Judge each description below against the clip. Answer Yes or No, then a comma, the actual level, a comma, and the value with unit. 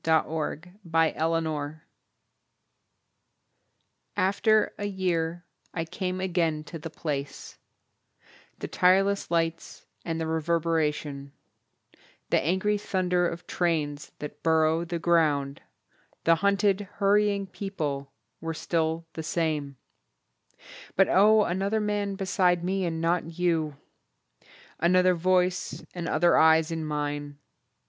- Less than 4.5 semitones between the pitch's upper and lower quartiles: Yes, average, 2.8 semitones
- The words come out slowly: Yes, slow, 110 wpm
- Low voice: No, medium, 170 Hz